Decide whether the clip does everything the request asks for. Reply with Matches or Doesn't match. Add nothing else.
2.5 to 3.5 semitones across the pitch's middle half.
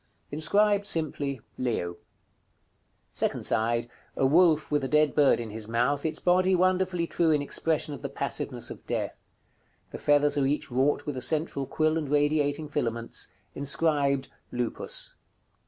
Matches